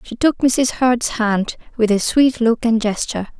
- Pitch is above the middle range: Yes, high, 230 Hz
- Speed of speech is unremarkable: Yes, average, 195 wpm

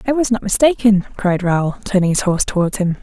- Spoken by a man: No, female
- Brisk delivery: Yes, fast, 220 wpm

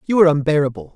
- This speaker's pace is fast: No, average, 190 wpm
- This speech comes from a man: Yes, male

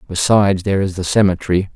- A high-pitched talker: No, very low, 95 Hz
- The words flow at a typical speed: Yes, average, 170 wpm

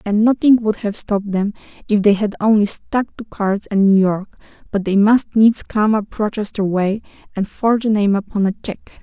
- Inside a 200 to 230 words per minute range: Yes, fast, 205 wpm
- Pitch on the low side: No, high, 210 Hz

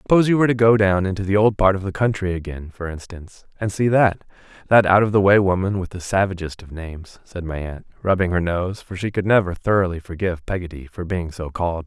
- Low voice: Yes, very low, 95 Hz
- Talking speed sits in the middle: No, fast, 235 wpm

